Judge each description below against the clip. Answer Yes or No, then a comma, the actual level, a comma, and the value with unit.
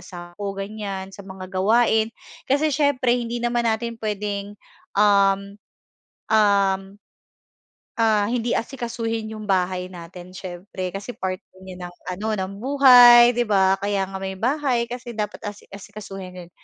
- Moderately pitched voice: No, high, 205 Hz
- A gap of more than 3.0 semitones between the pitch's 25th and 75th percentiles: Yes, average, 3.5 semitones